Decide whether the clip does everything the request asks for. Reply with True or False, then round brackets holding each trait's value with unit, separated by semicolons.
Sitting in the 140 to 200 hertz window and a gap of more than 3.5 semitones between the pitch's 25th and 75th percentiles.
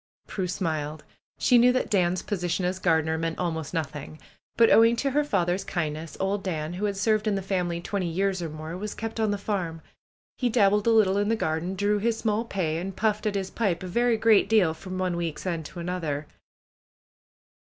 True (185 Hz; 4.0 semitones)